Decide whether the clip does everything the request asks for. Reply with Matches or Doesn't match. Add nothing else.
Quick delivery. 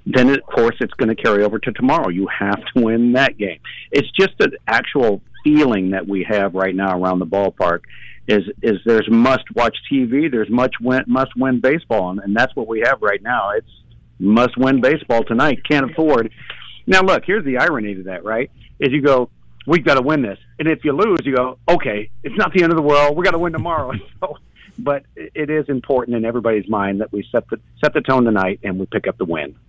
Matches